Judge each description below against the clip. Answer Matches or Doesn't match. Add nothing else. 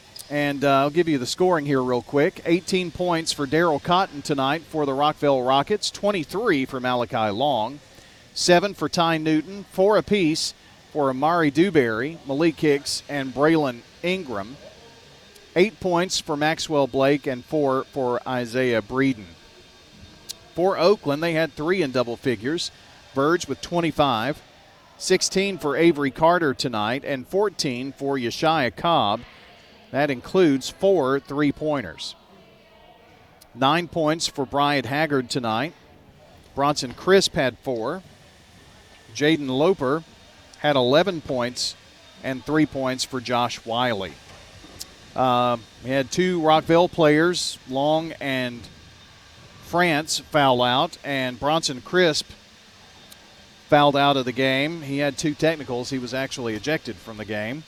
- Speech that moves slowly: Matches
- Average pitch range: Matches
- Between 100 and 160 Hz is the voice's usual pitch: Matches